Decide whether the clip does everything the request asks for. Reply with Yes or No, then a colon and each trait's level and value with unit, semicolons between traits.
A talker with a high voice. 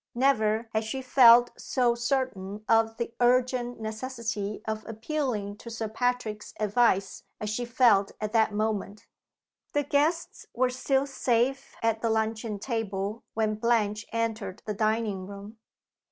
Yes: high, 225 Hz